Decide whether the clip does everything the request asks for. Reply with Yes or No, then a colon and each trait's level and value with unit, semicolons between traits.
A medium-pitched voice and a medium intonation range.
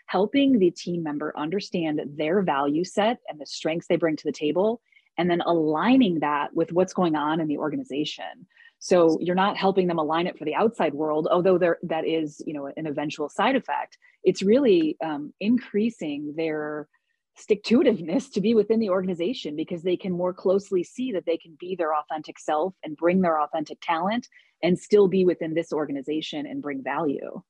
Yes: medium, 170 Hz; average, 4.7 semitones